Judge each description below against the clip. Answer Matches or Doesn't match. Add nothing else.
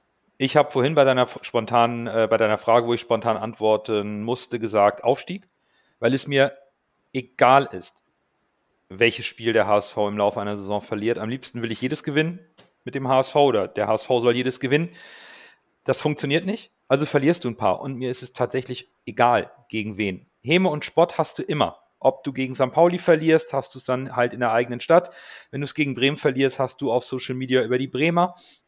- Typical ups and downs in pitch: Matches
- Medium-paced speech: Doesn't match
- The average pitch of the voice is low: Matches